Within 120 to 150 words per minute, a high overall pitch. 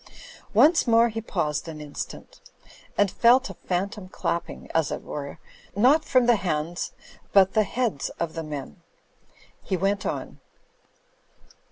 Yes: average, 145 wpm; high, 195 Hz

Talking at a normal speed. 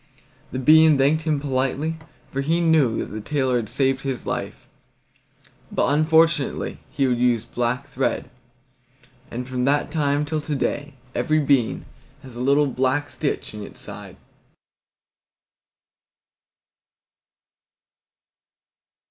No: slow, 120 wpm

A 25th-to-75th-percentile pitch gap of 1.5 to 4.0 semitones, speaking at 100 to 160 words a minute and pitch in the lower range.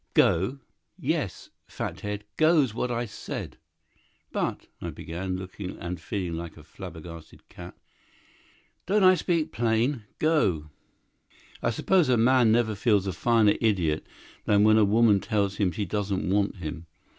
No: average, 4.6 semitones; average, 140 wpm; low, 105 Hz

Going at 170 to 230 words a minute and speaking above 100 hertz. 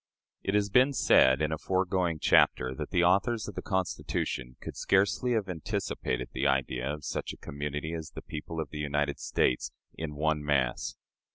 No: average, 180 wpm; very low, 80 Hz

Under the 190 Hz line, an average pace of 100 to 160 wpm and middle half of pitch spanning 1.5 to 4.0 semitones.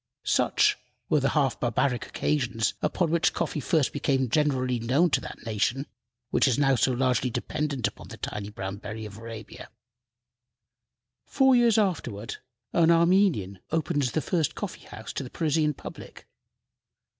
No: low, 135 Hz; average, 150 wpm; wide, 5.4 semitones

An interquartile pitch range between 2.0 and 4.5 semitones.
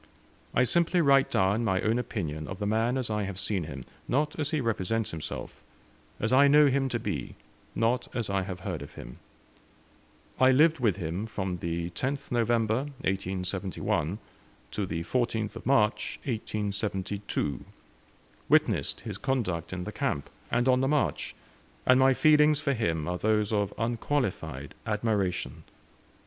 No: wide, 5.5 semitones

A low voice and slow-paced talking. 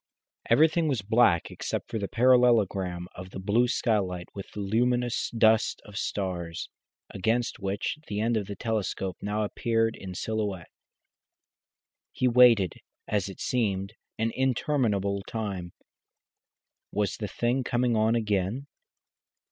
Yes: low, 110 Hz; slow, 125 wpm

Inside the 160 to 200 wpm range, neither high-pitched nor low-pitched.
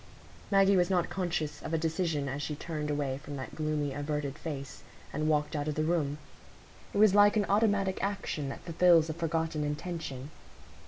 Yes: average, 180 wpm; medium, 155 Hz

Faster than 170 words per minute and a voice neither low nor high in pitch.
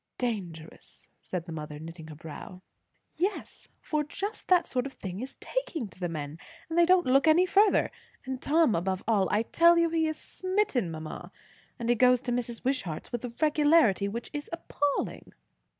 No: average, 180 wpm; very high, 250 Hz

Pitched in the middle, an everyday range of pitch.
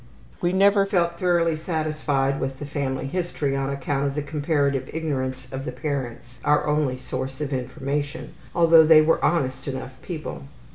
Yes: medium, 145 Hz; average, 3.3 semitones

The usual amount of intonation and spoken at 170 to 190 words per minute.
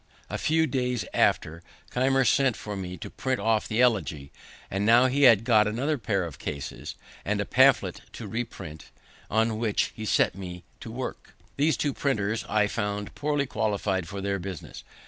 Yes: average, 4.3 semitones; average, 175 wpm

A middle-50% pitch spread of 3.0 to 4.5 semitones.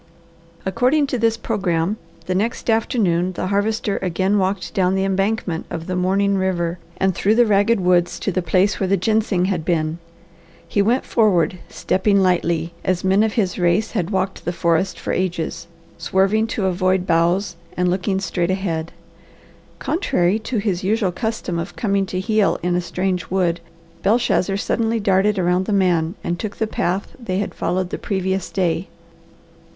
No: narrow, 2.5 semitones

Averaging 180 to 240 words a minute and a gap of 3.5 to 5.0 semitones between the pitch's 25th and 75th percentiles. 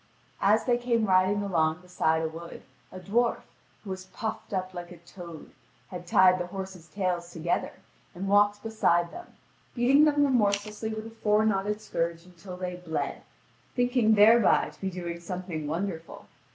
No: average, 165 wpm; average, 3.8 semitones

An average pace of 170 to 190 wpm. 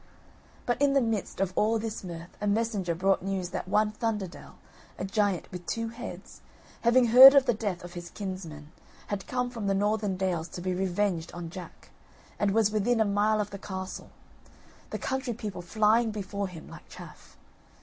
Yes: average, 185 wpm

